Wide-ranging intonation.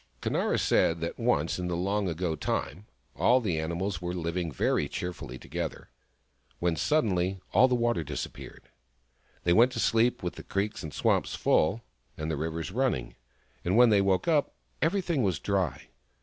Yes: wide, 5.7 semitones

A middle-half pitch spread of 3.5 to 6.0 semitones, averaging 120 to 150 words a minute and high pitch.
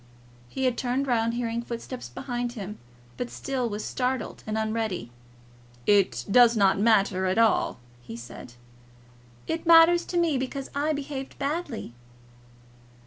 Yes: average, 4.2 semitones; average, 140 wpm; high, 240 Hz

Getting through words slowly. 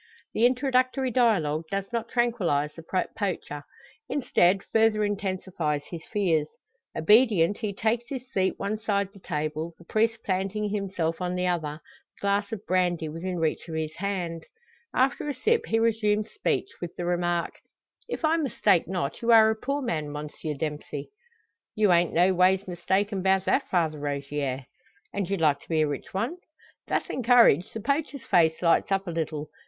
No: average, 170 wpm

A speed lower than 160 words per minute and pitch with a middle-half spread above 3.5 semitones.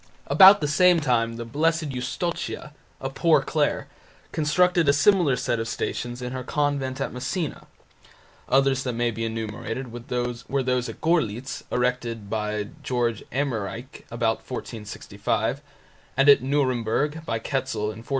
Yes: average, 140 wpm; average, 4.0 semitones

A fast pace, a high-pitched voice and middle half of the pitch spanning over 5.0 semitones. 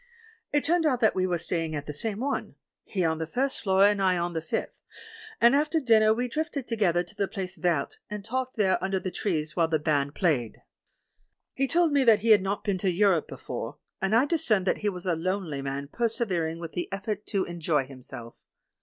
Yes: fast, 220 wpm; high, 195 Hz; wide, 5.4 semitones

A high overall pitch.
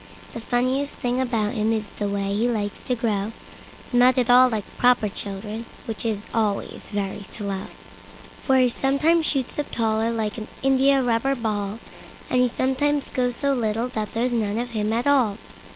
Yes: high, 230 Hz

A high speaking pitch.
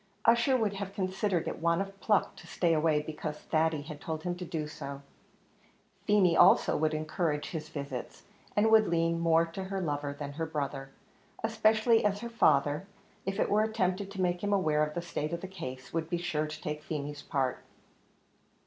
No: medium, 165 Hz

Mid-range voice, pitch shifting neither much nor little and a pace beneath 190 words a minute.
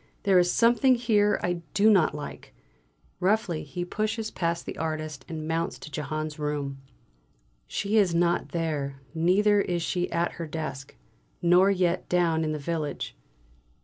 Yes: medium, 170 Hz; average, 3.8 semitones; average, 150 wpm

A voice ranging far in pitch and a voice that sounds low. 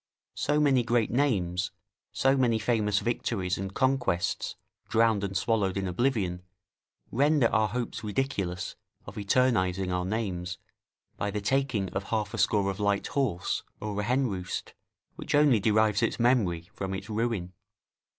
No: average, 4.1 semitones; low, 105 Hz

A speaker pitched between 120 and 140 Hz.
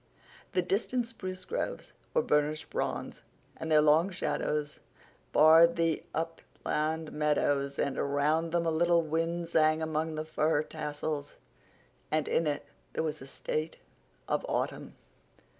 No: medium, 155 Hz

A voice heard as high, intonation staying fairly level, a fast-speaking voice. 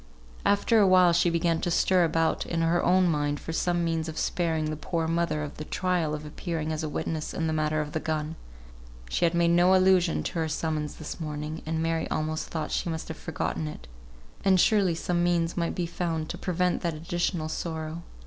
No: medium, 165 Hz; narrow, 1.8 semitones; fast, 210 wpm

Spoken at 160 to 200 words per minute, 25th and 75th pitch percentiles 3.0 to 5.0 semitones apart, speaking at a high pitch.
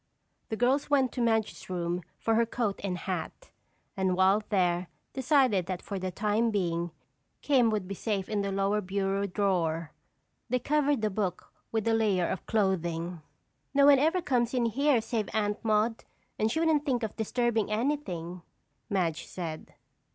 Yes: average, 165 wpm; average, 4.3 semitones; high, 210 Hz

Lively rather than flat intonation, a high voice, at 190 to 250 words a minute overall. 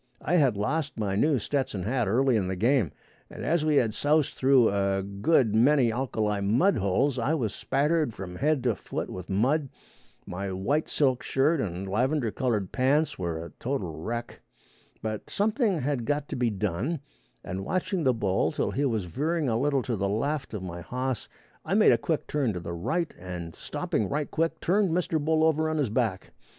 No: wide, 6.9 semitones; low, 125 Hz; average, 195 wpm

